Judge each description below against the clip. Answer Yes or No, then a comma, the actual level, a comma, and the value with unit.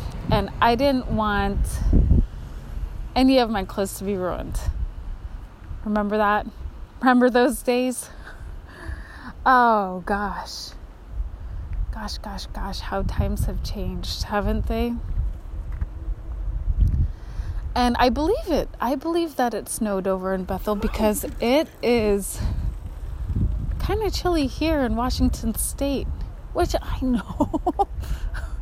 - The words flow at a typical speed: No, slow, 110 wpm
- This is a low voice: No, high, 200 Hz